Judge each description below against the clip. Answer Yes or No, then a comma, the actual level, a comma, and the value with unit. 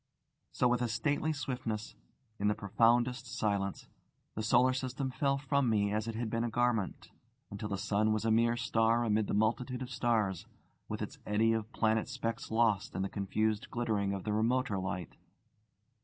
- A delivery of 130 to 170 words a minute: No, average, 180 wpm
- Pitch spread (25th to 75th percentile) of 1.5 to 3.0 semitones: Yes, average, 2.7 semitones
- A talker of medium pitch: No, low, 115 Hz